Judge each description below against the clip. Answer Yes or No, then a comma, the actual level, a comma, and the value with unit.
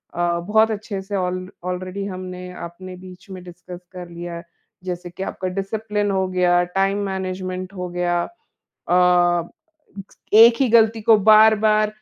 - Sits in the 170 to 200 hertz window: Yes, medium, 185 Hz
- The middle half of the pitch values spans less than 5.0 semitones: Yes, narrow, 2.6 semitones